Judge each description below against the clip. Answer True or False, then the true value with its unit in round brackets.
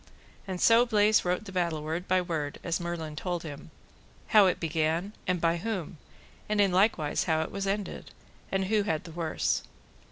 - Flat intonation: False (3.4 semitones)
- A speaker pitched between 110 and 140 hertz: False (180 Hz)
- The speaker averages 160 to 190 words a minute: True (185 wpm)